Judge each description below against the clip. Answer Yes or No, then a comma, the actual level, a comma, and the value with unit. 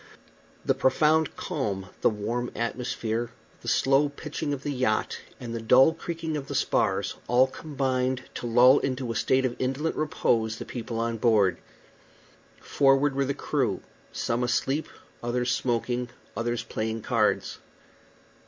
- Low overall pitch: Yes, low, 125 Hz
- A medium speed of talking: Yes, average, 145 wpm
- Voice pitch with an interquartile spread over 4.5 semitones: No, average, 2.8 semitones